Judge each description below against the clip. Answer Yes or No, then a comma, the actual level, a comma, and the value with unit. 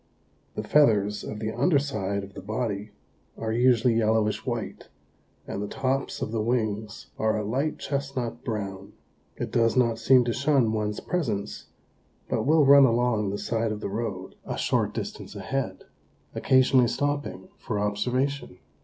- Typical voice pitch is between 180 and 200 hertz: No, low, 115 Hz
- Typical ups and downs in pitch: Yes, average, 3.7 semitones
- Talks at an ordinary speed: Yes, average, 155 wpm